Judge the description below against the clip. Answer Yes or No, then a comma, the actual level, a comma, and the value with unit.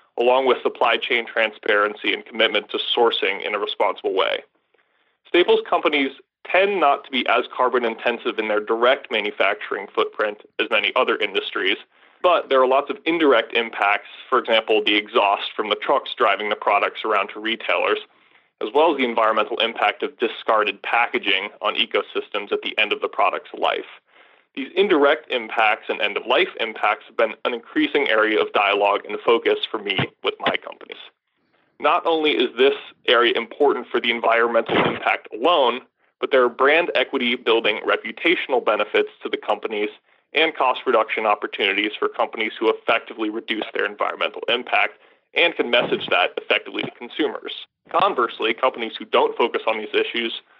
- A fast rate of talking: No, average, 165 wpm